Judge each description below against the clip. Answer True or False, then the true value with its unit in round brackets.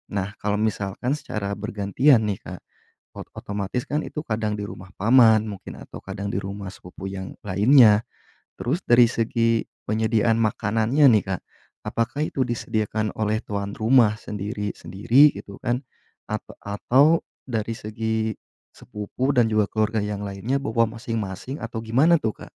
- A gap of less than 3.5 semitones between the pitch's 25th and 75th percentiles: True (2.7 semitones)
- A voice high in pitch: False (110 Hz)